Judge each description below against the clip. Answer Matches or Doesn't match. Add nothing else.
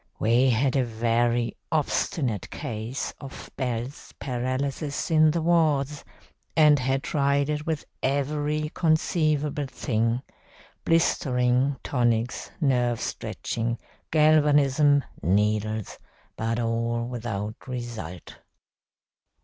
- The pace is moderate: Doesn't match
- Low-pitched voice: Matches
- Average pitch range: Matches